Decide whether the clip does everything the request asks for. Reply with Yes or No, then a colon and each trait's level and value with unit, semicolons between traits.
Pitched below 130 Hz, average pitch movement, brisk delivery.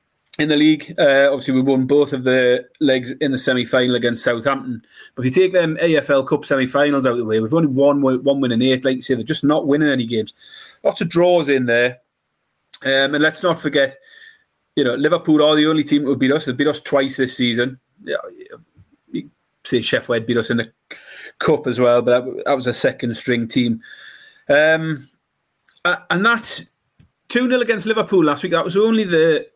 No: medium, 140 Hz; average, 4.0 semitones; fast, 215 wpm